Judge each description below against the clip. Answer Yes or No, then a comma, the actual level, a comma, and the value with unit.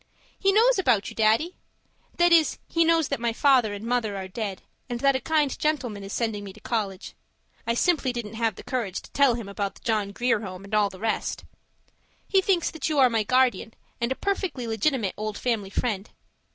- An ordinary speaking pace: No, fast, 210 wpm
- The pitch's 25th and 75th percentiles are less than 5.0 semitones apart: No, average, 5.3 semitones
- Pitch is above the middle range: Yes, high, 235 Hz